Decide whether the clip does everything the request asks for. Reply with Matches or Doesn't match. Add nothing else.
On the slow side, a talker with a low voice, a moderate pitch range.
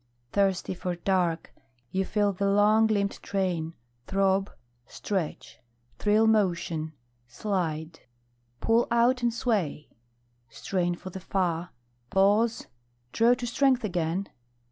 Doesn't match